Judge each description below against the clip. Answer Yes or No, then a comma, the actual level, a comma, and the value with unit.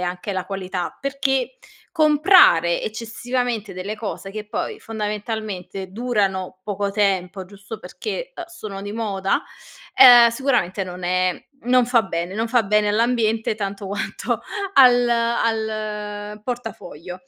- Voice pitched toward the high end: Yes, high, 210 Hz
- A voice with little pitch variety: No, average, 3.6 semitones